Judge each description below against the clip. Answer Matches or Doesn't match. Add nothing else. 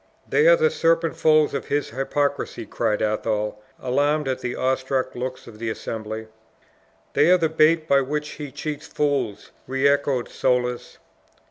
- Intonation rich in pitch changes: Doesn't match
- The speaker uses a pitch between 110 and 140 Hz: Matches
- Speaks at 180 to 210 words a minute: Doesn't match